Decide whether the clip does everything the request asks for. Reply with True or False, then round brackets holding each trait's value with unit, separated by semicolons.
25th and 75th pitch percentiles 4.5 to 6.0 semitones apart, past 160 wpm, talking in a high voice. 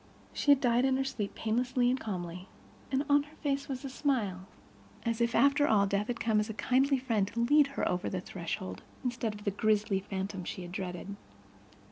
True (5.3 semitones; 200 wpm; 225 Hz)